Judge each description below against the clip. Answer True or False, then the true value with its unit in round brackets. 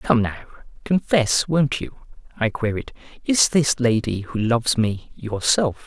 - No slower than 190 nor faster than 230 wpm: False (145 wpm)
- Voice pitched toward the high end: False (125 Hz)